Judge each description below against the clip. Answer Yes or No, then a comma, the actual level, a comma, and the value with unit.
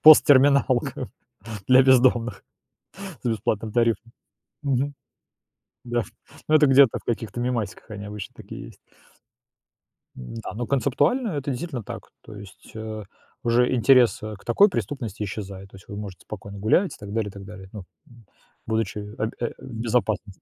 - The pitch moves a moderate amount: Yes, average, 3.6 semitones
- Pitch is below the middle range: Yes, low, 115 Hz